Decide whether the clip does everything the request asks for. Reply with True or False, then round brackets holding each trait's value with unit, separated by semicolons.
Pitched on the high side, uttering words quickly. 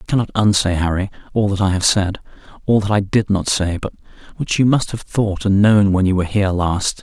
False (100 Hz; 230 wpm)